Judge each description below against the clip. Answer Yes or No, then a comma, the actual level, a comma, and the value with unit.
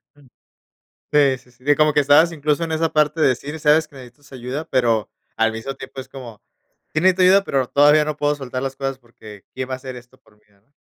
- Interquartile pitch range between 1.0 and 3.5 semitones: Yes, average, 2.9 semitones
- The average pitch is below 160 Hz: Yes, low, 135 Hz